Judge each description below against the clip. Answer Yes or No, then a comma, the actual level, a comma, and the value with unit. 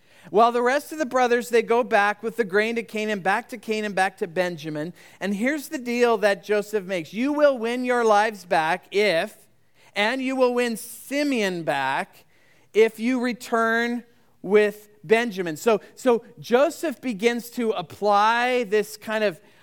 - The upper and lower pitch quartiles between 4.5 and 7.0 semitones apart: No, average, 2.9 semitones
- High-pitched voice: Yes, high, 225 Hz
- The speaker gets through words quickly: No, average, 165 wpm